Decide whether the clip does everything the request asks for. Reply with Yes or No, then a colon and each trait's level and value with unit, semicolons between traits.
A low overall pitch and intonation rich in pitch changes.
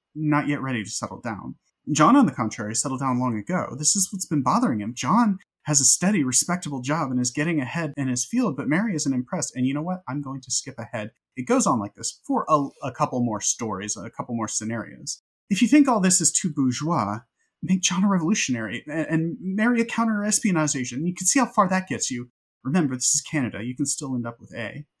No: medium, 145 Hz; wide, 6.7 semitones